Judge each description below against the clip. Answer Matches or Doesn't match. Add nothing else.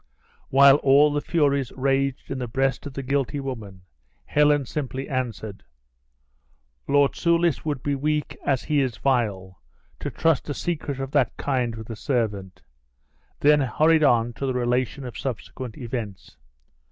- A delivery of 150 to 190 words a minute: Matches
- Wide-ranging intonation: Doesn't match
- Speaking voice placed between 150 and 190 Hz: Doesn't match